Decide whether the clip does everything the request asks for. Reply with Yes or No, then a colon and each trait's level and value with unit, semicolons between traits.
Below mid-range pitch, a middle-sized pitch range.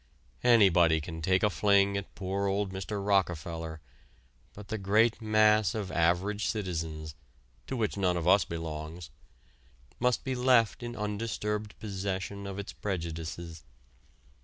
Yes: low, 100 Hz; average, 3.8 semitones